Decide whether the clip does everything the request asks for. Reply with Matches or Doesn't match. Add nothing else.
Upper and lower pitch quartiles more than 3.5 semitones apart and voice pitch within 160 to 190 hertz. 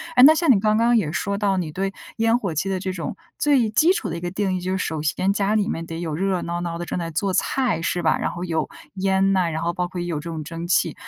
Doesn't match